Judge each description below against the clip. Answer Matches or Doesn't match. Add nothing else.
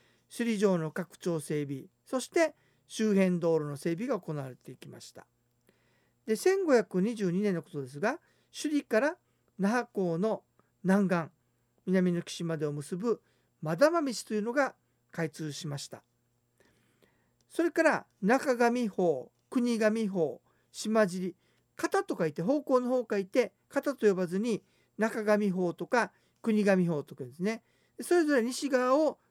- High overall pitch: Matches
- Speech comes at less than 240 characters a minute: Matches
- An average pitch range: Doesn't match